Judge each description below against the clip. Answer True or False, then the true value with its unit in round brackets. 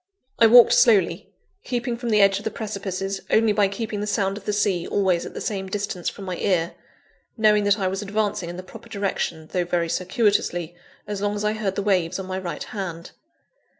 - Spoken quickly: True (215 wpm)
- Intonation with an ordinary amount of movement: False (2.2 semitones)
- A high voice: True (200 Hz)